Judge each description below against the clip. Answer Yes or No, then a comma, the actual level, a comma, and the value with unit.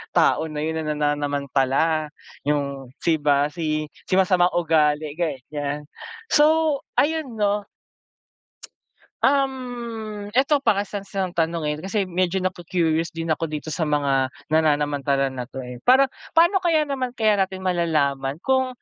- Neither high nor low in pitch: Yes, medium, 165 Hz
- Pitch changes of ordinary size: No, wide, 6.3 semitones